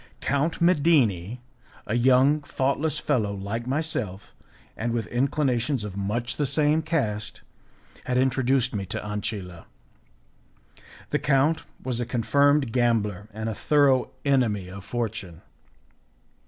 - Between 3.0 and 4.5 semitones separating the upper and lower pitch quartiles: No, average, 5.1 semitones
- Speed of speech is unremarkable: No, slow, 120 wpm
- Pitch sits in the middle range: No, low, 120 Hz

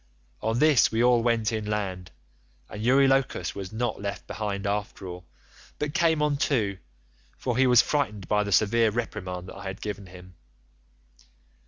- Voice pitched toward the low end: Yes, low, 105 Hz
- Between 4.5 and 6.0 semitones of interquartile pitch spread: No, average, 3.9 semitones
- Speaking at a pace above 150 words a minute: Yes, average, 160 wpm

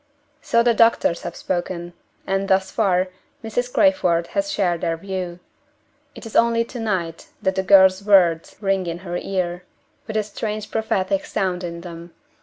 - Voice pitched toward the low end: No, high, 190 Hz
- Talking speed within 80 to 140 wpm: No, average, 165 wpm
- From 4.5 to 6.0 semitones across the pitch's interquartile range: No, average, 3.6 semitones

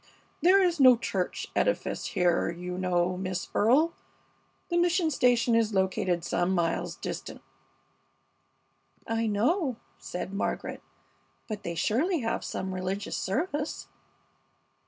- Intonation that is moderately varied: No, wide, 8.2 semitones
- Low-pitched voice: No, high, 215 Hz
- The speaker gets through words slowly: Yes, slow, 115 wpm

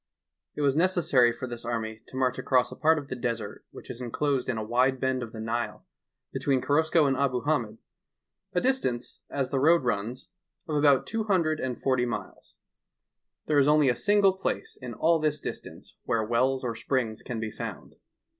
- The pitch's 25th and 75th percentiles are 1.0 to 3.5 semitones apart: No, average, 4.0 semitones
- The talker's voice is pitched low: Yes, low, 130 Hz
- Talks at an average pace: Yes, average, 190 wpm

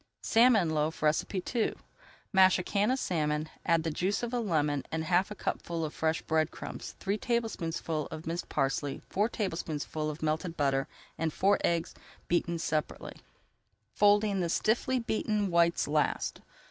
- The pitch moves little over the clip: No, average, 4.6 semitones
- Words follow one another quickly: No, average, 160 wpm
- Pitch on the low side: No, medium, 170 Hz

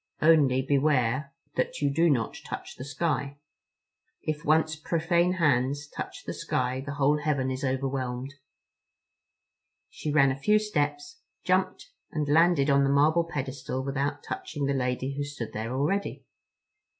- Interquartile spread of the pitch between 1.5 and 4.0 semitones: Yes, average, 2.8 semitones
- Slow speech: No, average, 145 wpm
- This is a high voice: No, medium, 140 Hz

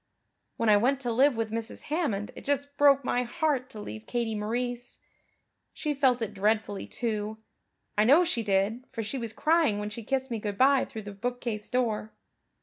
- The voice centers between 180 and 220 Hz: No, high, 235 Hz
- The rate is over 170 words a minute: Yes, average, 190 wpm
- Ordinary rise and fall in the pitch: Yes, average, 4.0 semitones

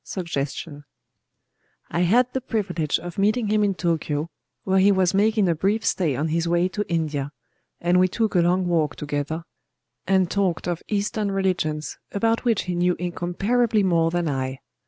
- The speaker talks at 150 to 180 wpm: Yes, average, 165 wpm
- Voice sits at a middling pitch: Yes, medium, 180 Hz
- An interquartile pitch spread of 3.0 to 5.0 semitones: Yes, average, 3.6 semitones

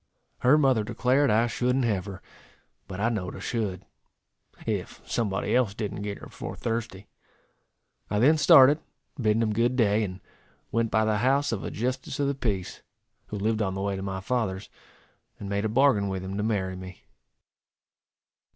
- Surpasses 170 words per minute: Yes, average, 180 wpm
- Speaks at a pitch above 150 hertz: No, low, 110 Hz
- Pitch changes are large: No, average, 4.0 semitones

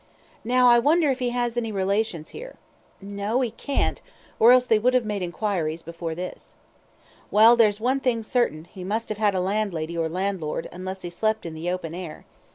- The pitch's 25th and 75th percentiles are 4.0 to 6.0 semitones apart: Yes, average, 5.1 semitones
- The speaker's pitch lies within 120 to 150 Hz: No, high, 205 Hz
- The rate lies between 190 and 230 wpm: Yes, average, 195 wpm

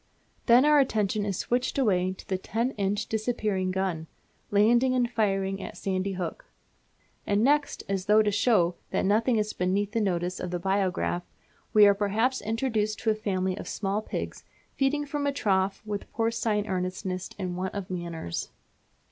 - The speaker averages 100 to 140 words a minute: No, average, 170 wpm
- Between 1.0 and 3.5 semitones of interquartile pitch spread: Yes, average, 3.2 semitones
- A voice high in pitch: Yes, high, 205 Hz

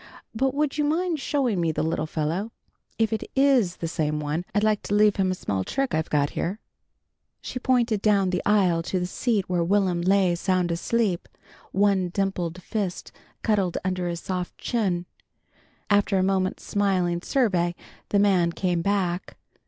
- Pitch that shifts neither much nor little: Yes, average, 3.4 semitones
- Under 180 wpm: Yes, average, 170 wpm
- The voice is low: No, high, 190 Hz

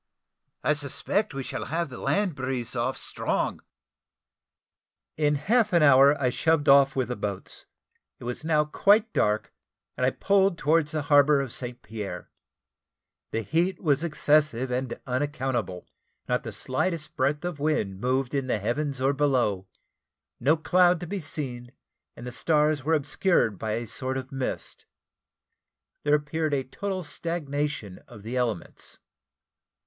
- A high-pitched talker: No, medium, 140 Hz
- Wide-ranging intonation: No, average, 3.8 semitones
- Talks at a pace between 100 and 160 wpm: Yes, average, 150 wpm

